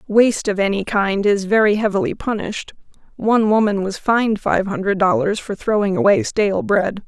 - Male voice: No, female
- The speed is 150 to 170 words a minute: Yes, average, 160 wpm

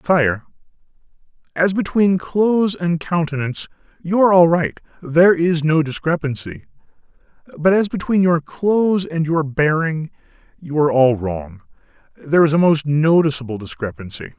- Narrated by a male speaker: Yes, male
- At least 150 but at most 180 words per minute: No, slow, 135 wpm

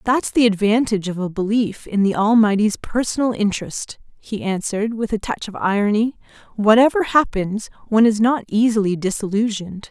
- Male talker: No, female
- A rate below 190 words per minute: Yes, average, 150 wpm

